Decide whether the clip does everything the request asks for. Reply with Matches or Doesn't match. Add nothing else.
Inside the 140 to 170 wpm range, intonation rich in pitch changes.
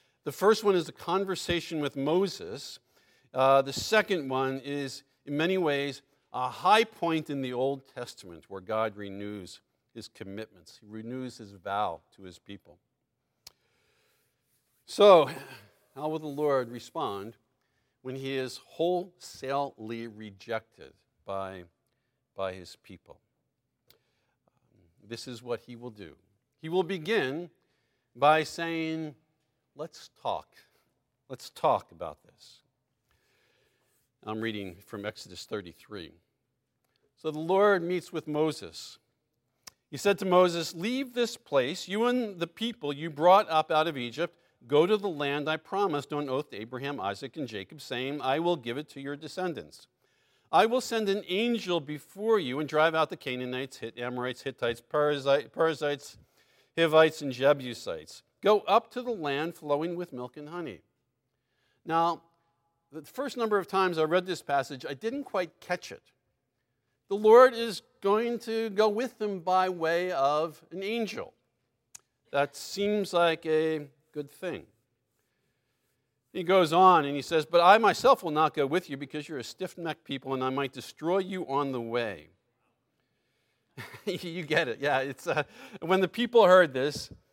Matches